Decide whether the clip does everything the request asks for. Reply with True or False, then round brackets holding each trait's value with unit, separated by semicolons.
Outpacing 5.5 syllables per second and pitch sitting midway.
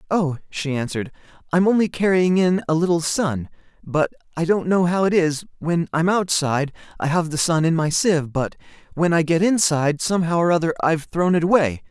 True (5.7 syllables/s; 165 Hz)